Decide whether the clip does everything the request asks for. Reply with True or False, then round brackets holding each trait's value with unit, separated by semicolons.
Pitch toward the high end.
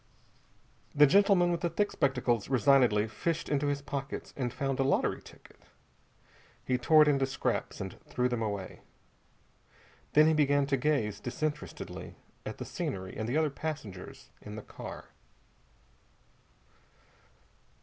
False (135 Hz)